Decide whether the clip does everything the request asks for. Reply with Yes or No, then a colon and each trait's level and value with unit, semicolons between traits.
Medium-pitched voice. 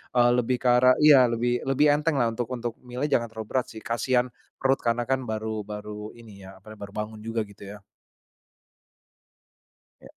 No: low, 120 Hz